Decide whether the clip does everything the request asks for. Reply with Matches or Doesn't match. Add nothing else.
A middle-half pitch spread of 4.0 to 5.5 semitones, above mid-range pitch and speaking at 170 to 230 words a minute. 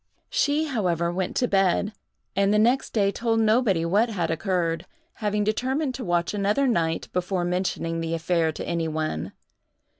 Doesn't match